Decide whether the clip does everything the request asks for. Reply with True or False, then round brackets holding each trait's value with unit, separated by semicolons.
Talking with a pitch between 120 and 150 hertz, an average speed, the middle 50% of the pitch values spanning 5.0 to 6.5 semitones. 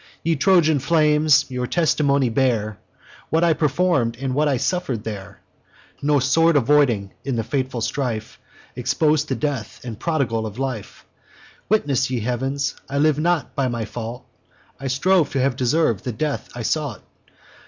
False (135 Hz; 155 wpm; 4.2 semitones)